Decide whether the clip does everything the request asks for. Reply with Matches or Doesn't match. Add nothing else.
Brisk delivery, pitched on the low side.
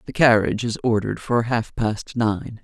Doesn't match